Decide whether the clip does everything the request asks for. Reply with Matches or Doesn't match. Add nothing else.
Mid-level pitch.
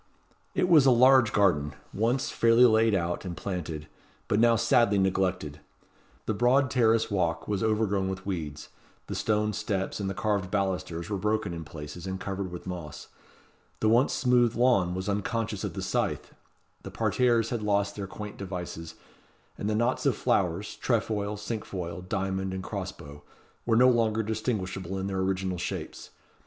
Doesn't match